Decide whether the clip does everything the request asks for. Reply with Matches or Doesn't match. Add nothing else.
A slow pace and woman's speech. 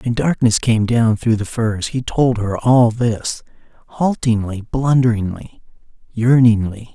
Doesn't match